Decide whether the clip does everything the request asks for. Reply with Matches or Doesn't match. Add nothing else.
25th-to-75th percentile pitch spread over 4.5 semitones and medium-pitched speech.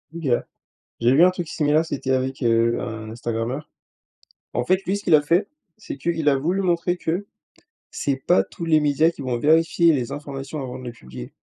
Matches